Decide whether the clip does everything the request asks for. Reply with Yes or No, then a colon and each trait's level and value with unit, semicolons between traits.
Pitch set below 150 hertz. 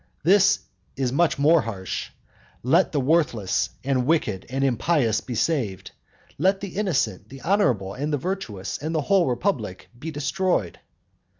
Yes: medium, 140 Hz